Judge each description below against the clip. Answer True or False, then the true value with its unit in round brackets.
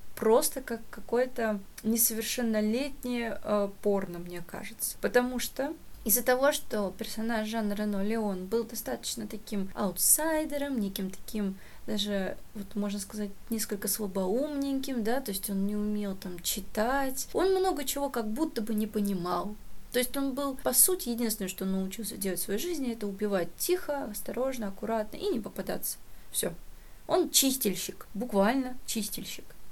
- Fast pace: False (145 wpm)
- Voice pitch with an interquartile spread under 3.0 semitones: False (4.2 semitones)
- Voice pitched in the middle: False (225 Hz)